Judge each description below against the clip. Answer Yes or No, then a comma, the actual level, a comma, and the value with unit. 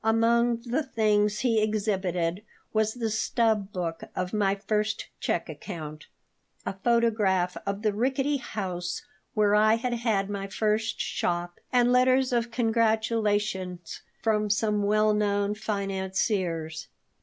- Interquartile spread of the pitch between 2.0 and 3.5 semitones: Yes, average, 2.7 semitones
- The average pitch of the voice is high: Yes, high, 210 Hz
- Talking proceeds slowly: Yes, slow, 125 wpm